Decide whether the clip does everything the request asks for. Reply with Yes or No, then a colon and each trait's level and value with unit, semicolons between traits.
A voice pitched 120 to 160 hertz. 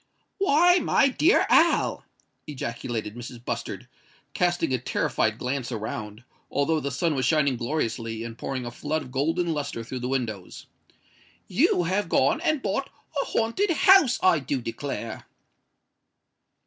Yes: medium, 140 Hz